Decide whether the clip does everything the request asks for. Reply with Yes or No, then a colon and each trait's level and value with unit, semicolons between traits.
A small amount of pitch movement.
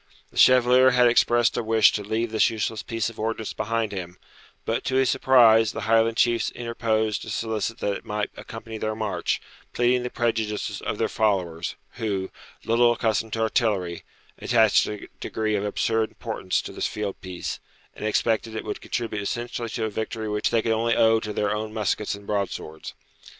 Yes: narrow, 1.7 semitones